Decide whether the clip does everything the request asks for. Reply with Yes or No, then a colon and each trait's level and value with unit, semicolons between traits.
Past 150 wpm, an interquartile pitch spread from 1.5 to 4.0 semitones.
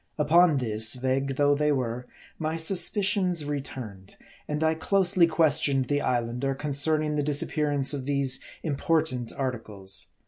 No: average, 140 wpm; average, 3.6 semitones